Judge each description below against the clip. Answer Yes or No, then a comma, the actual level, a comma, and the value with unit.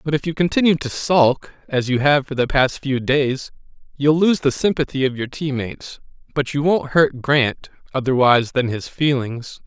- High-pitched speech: No, medium, 140 Hz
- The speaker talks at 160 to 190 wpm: Yes, average, 180 wpm